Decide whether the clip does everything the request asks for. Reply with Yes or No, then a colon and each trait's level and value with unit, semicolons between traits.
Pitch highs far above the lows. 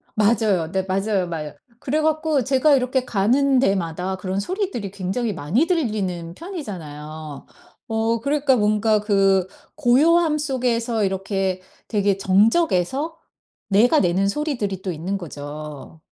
Yes: wide, 5.9 semitones